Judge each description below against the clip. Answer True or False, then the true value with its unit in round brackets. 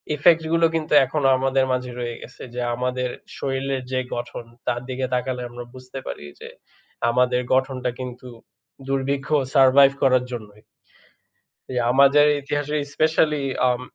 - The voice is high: False (130 Hz)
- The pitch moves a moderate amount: False (1.8 semitones)